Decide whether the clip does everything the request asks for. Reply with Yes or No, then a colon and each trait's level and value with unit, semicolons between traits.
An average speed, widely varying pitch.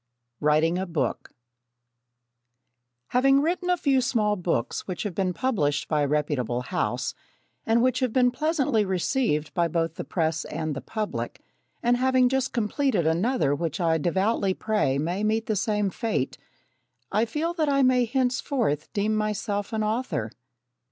Yes: average, 155 wpm; wide, 7.4 semitones